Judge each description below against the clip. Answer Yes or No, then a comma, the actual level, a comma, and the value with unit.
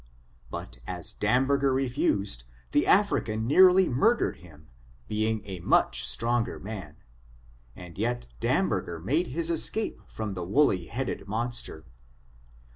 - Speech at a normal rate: No, slow, 120 wpm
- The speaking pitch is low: Yes, low, 110 Hz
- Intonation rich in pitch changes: Yes, wide, 6.2 semitones